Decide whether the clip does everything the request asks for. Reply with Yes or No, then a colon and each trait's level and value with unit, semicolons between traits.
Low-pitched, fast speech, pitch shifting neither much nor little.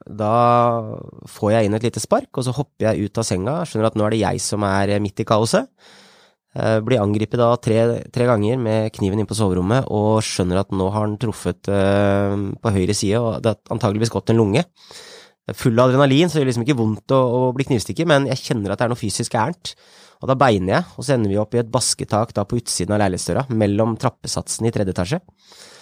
Yes: low, 110 Hz; fast, 225 wpm; average, 3.3 semitones